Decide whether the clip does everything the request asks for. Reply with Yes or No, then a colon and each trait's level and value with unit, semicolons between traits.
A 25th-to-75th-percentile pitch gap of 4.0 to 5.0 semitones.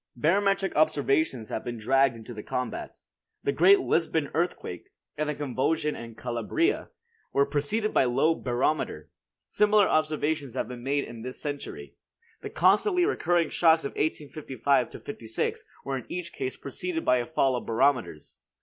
Yes: average, 4.7 semitones